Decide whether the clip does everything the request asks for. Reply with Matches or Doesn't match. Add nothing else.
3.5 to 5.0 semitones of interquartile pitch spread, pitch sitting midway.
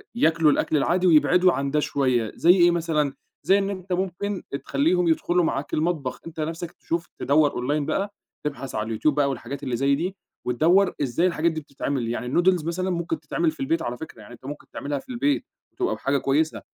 Matches